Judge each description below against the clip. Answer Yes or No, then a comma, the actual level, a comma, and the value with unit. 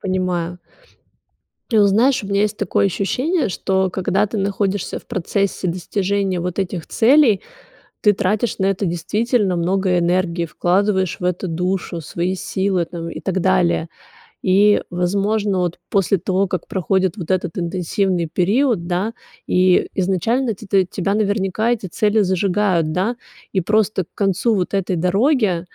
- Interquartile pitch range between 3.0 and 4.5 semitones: No, narrow, 2.4 semitones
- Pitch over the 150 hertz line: Yes, high, 190 Hz